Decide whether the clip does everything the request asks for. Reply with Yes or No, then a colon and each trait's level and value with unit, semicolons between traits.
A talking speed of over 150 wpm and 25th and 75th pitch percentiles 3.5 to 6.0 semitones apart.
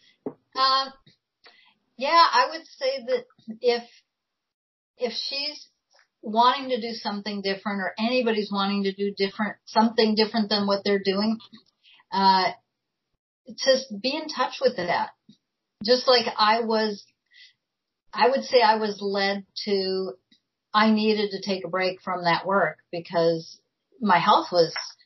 No: slow, 135 wpm; average, 4.3 semitones